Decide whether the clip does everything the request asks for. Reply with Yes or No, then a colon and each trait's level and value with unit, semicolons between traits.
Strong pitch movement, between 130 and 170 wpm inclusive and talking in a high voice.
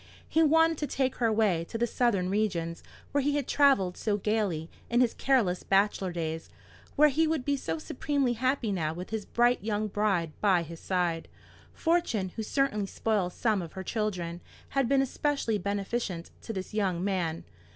No: wide, 6.0 semitones; average, 180 wpm; high, 210 Hz